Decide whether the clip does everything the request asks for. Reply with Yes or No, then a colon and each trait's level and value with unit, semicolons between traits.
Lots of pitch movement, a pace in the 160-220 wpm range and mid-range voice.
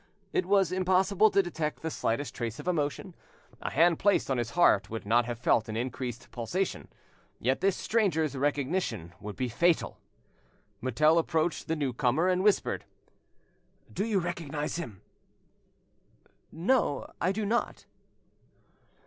No: wide, 6.8 semitones; average, 140 wpm; medium, 155 Hz